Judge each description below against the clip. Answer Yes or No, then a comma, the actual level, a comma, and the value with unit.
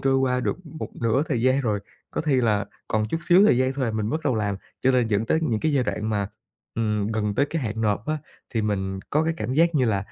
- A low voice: Yes, low, 115 Hz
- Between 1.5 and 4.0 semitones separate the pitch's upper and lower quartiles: No, average, 4.5 semitones